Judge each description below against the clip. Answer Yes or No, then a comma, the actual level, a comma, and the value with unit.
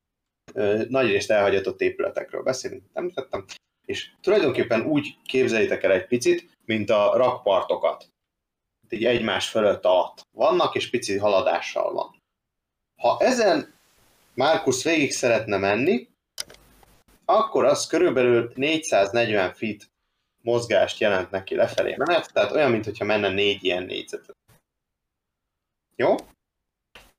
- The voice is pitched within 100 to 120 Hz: No, low, 130 Hz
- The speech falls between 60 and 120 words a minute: Yes, average, 110 wpm